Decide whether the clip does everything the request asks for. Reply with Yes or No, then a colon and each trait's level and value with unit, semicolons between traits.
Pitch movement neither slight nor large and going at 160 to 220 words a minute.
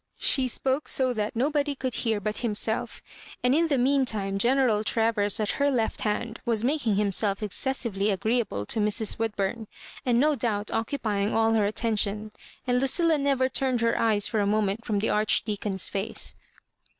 Yes: average, 3.7 semitones; average, 175 wpm